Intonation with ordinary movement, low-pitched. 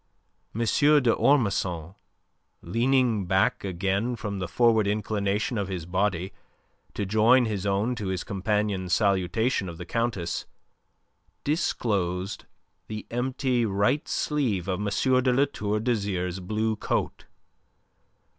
Yes: average, 3.8 semitones; low, 105 Hz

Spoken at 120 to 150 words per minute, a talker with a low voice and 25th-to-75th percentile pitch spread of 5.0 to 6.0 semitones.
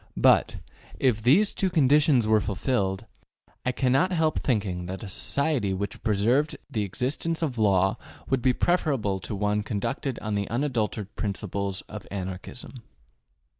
Yes: average, 140 wpm; low, 110 Hz; wide, 5.4 semitones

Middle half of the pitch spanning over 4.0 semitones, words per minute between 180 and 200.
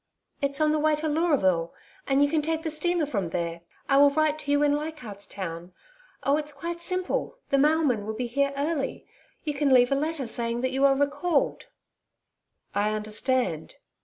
Yes: average, 4.6 semitones; average, 190 wpm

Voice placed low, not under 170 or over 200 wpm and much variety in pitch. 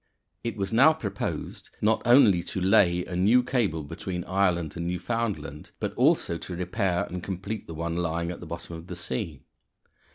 No: very low, 90 Hz; average, 175 wpm; average, 3.4 semitones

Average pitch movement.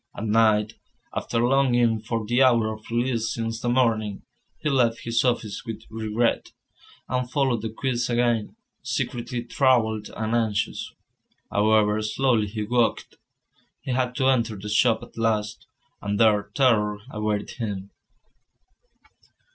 No: narrow, 2.1 semitones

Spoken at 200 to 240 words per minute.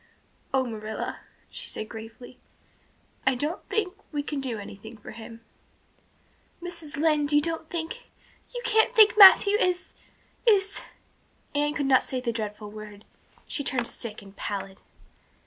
No: average, 145 wpm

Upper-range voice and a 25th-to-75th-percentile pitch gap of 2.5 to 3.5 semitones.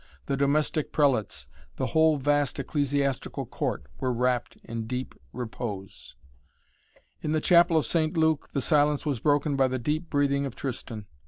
No: medium, 140 Hz; average, 3.1 semitones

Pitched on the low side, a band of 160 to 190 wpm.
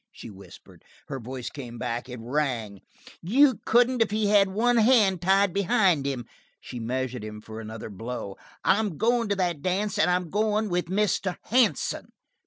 No: medium, 180 Hz; average, 170 wpm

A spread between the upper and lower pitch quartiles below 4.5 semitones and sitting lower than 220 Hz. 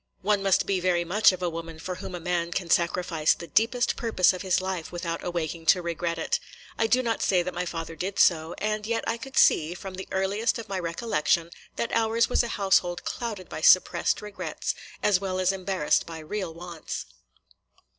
Yes: average, 3.3 semitones; medium, 185 Hz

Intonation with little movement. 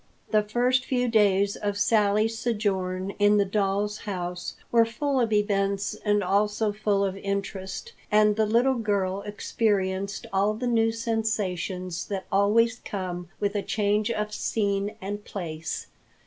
Yes: narrow, 2.0 semitones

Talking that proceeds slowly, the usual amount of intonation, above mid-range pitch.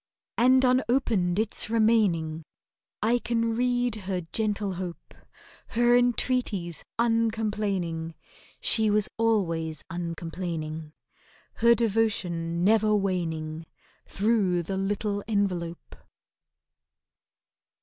Yes: slow, 85 wpm; average, 4.8 semitones; high, 205 Hz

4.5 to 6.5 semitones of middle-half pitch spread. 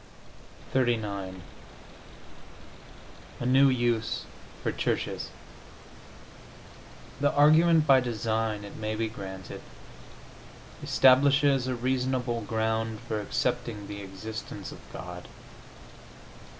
No: average, 3.8 semitones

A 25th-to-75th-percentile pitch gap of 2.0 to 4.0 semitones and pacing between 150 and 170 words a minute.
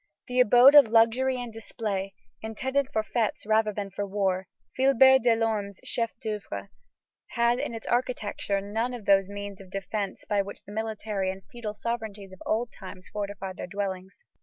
Yes: average, 3.0 semitones; average, 165 wpm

